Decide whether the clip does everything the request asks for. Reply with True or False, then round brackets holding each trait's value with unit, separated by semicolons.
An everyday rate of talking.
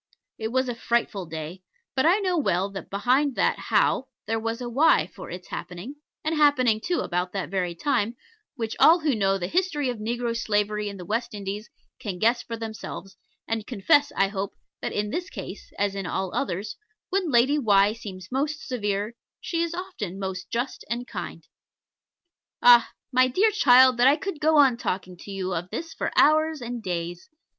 True (190 wpm)